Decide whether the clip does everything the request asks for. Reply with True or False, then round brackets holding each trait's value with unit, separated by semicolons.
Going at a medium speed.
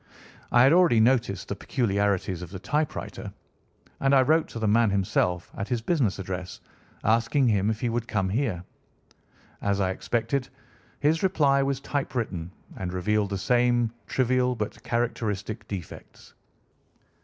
True (145 wpm)